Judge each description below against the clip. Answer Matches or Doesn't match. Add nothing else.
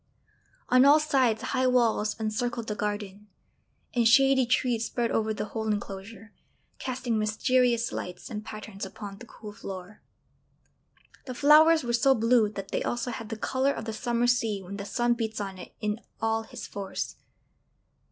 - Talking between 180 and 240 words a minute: Doesn't match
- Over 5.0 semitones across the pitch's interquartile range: Doesn't match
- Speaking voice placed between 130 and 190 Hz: Doesn't match